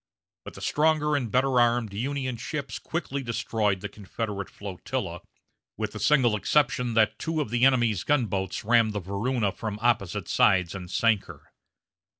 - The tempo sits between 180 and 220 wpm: No, average, 155 wpm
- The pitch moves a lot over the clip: No, average, 4.4 semitones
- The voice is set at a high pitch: No, low, 115 Hz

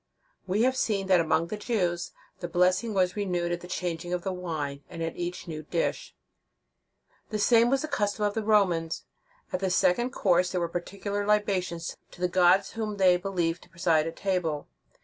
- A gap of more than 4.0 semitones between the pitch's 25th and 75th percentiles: No, average, 2.9 semitones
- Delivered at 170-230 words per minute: Yes, average, 190 wpm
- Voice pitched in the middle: Yes, medium, 180 Hz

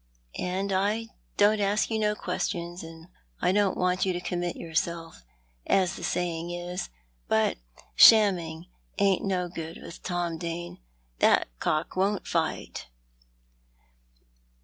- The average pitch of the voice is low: No, medium, 180 Hz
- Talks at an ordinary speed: No, slow, 125 wpm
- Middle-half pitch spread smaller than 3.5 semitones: Yes, average, 2.7 semitones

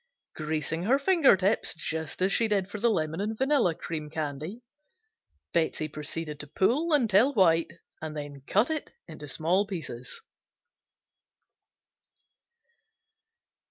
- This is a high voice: No, medium, 175 Hz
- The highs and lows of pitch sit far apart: Yes, wide, 6.1 semitones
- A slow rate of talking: Yes, slow, 125 wpm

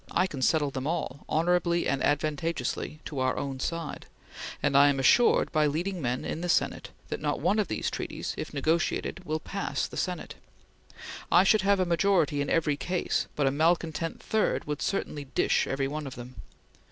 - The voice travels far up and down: No, average, 3.7 semitones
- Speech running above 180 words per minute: Yes, average, 190 wpm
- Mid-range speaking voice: Yes, medium, 155 Hz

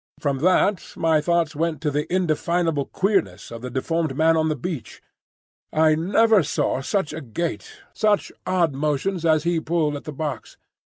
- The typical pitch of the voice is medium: Yes, medium, 160 Hz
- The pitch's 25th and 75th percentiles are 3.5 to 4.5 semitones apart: No, average, 2.8 semitones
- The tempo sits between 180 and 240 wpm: No, average, 170 wpm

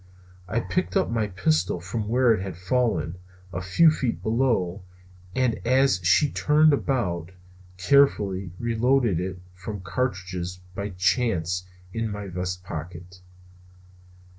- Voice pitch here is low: Yes, low, 100 Hz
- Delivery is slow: Yes, slow, 125 wpm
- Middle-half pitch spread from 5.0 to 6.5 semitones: Yes, wide, 5.4 semitones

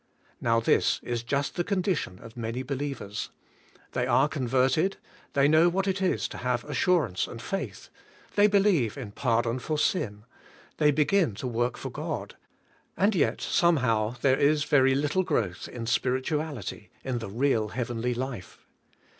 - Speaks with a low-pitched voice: Yes, low, 130 Hz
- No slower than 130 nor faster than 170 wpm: Yes, average, 155 wpm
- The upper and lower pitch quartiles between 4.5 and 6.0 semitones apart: Yes, average, 5.1 semitones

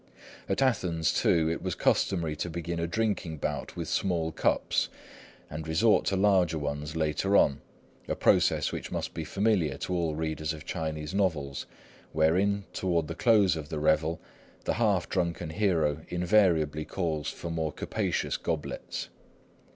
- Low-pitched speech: Yes, very low, 80 Hz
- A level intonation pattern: No, average, 3.3 semitones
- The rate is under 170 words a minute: Yes, average, 150 wpm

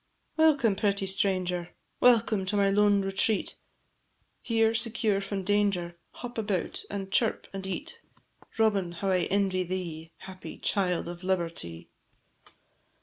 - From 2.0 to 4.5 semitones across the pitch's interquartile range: Yes, narrow, 2.4 semitones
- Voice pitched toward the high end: Yes, high, 195 Hz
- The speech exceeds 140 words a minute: No, slow, 135 wpm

